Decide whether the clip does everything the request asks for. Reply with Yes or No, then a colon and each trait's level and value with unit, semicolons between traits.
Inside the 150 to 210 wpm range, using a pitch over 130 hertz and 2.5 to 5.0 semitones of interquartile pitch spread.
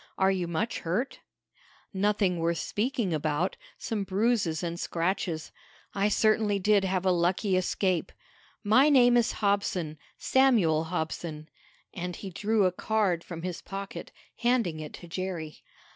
No: average, 140 wpm; high, 190 Hz; average, 3.7 semitones